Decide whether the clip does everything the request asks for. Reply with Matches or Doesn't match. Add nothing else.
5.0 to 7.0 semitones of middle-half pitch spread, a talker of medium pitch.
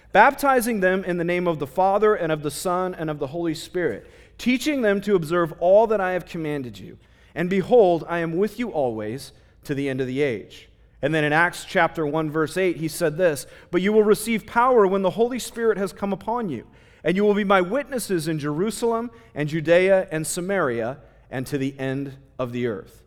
Matches